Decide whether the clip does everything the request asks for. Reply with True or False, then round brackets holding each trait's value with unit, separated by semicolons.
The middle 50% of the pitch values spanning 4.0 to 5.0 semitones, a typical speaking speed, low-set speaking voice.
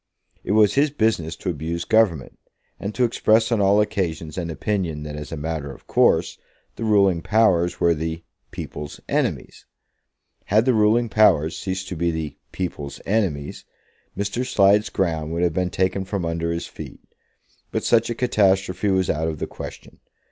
True (4.6 semitones; 170 wpm; 95 Hz)